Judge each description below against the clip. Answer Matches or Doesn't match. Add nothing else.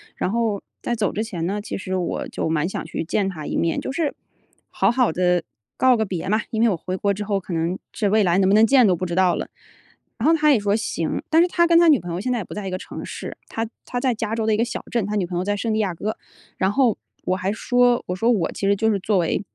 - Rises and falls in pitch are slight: Doesn't match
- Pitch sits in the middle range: Doesn't match